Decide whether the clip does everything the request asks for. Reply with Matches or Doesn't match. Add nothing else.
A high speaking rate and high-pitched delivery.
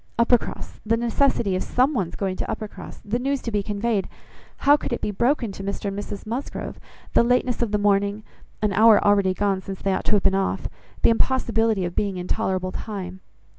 Matches